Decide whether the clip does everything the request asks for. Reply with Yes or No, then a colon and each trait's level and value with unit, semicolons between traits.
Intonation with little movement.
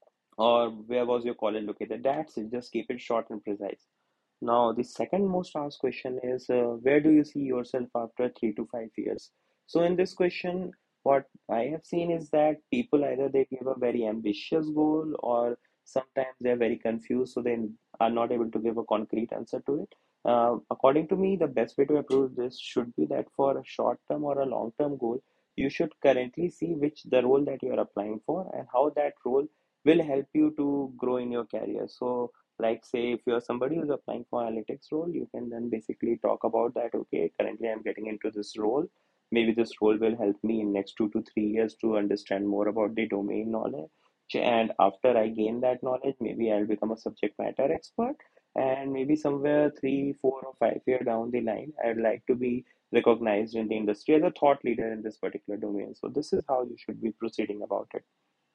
No: average, 3.8 semitones